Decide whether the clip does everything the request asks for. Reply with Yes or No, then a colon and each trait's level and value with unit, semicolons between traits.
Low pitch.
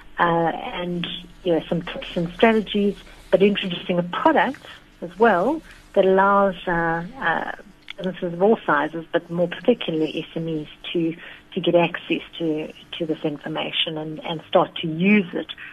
No: medium, 175 Hz